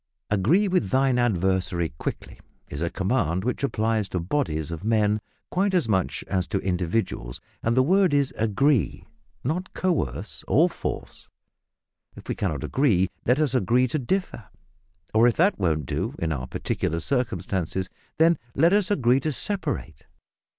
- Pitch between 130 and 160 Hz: No, low, 115 Hz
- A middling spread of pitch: No, wide, 7.7 semitones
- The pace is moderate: Yes, average, 155 wpm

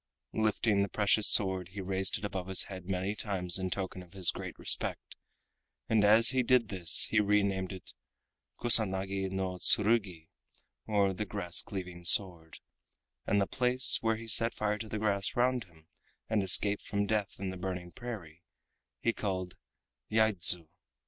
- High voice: No, low, 100 Hz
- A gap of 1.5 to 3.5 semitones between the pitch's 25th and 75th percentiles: Yes, narrow, 2.6 semitones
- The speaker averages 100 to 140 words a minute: No, average, 165 wpm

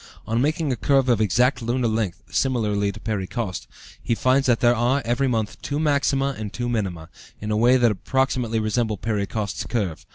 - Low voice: Yes, low, 115 Hz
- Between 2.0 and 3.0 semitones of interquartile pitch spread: No, average, 3.4 semitones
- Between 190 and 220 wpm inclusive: Yes, average, 195 wpm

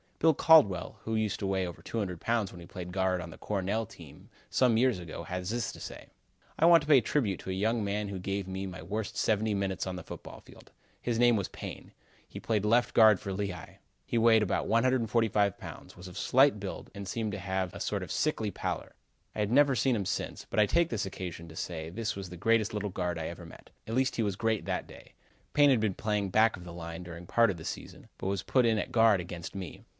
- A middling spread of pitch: Yes, average, 3.7 semitones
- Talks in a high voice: No, low, 100 Hz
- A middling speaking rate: No, fast, 245 wpm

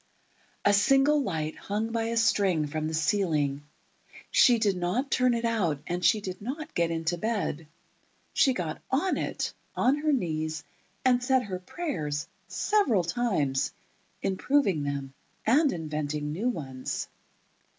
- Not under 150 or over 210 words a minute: No, slow, 135 wpm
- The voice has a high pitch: Yes, high, 195 Hz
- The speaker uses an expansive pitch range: Yes, wide, 7.8 semitones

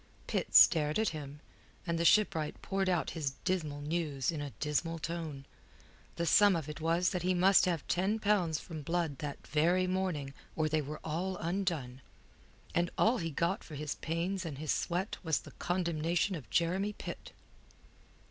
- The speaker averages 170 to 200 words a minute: Yes, average, 175 wpm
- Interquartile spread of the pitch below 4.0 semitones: Yes, average, 3.2 semitones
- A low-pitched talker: No, medium, 165 Hz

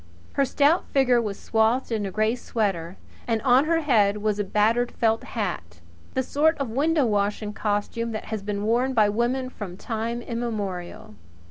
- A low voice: No, high, 225 Hz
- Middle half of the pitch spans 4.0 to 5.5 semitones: No, average, 3.3 semitones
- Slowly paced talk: No, average, 170 wpm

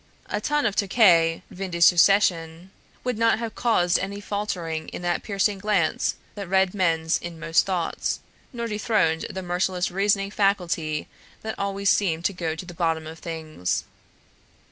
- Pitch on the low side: No, medium, 185 Hz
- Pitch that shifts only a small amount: No, average, 3.5 semitones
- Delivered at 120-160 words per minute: Yes, average, 155 wpm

